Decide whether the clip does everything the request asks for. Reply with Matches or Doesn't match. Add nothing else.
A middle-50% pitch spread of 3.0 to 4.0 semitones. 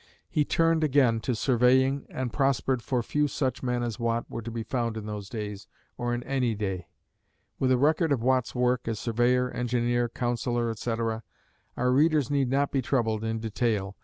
Doesn't match